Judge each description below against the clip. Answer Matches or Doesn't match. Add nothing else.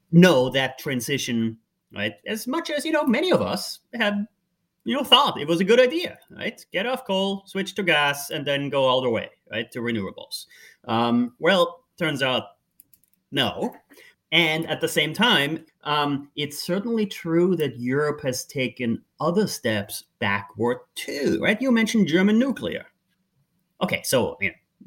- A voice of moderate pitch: Matches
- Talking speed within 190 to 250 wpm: Doesn't match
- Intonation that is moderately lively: Doesn't match